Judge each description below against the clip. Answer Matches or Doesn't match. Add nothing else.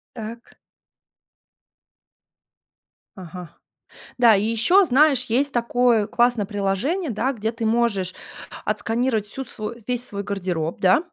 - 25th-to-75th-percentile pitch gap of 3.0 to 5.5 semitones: Matches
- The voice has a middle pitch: Doesn't match